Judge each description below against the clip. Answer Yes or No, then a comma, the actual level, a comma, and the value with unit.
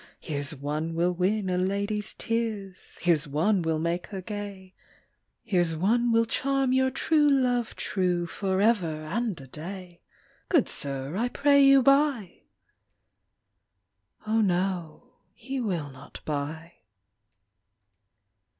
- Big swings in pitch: Yes, wide, 5.8 semitones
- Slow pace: Yes, slow, 130 wpm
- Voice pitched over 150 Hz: Yes, high, 190 Hz